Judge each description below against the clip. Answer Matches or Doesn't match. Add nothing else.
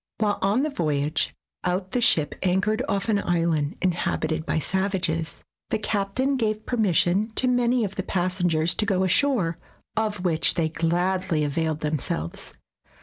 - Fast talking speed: Doesn't match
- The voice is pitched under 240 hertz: Matches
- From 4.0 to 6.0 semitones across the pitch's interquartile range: Matches